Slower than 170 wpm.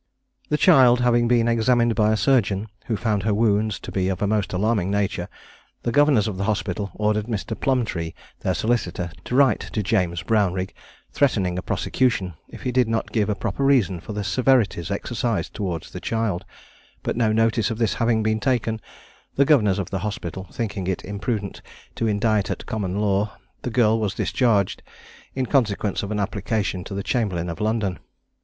No: average, 185 wpm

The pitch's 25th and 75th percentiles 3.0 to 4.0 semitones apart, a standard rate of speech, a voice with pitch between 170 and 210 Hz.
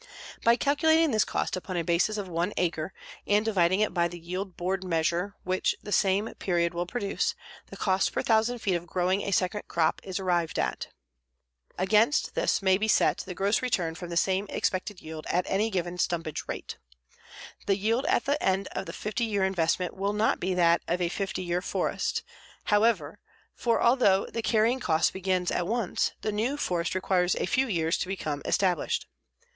Yes: average, 3.3 semitones; average, 190 wpm; high, 190 Hz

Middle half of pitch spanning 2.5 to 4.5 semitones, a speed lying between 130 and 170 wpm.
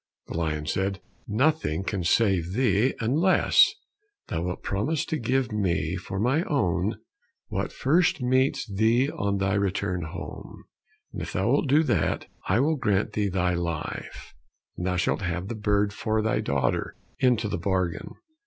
No: wide, 5.6 semitones; average, 160 wpm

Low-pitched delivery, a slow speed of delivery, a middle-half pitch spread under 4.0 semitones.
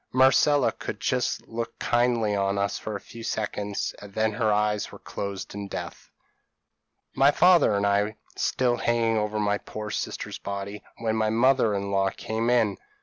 No: low, 110 Hz; average, 175 wpm; narrow, 2.5 semitones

